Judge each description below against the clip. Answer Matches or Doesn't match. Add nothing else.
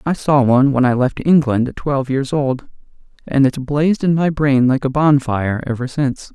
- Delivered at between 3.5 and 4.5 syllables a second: Doesn't match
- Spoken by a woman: Doesn't match